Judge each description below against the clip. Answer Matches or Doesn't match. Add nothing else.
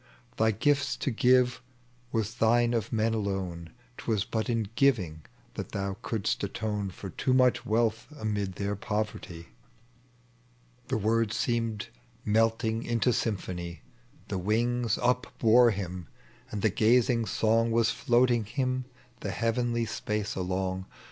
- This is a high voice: Doesn't match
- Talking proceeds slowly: Matches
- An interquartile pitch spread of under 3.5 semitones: Matches